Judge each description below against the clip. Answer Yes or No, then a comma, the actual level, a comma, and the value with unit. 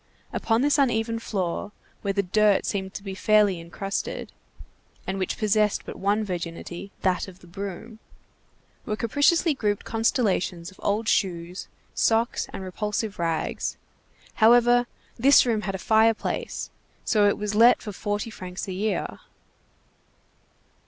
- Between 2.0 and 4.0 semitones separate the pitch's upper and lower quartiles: Yes, average, 2.8 semitones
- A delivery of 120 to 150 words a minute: Yes, average, 140 wpm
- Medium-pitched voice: No, high, 210 Hz